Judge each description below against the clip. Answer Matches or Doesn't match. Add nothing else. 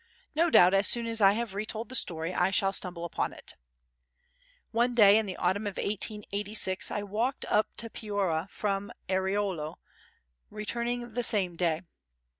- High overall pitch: Matches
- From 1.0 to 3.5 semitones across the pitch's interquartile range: Matches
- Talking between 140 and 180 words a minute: Matches